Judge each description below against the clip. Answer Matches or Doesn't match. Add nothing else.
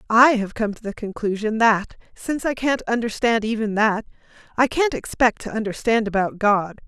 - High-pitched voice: Matches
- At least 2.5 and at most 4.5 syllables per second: Doesn't match